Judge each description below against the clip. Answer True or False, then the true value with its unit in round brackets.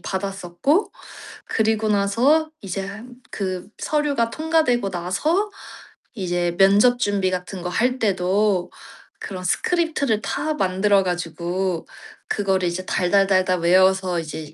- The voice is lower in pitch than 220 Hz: True (195 Hz)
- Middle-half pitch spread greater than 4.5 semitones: False (4.1 semitones)